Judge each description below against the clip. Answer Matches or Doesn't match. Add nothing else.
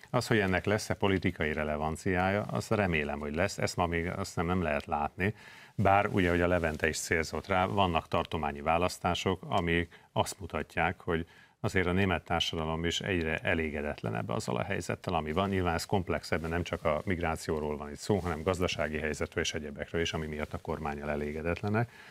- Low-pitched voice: Matches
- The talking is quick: Matches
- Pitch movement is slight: Doesn't match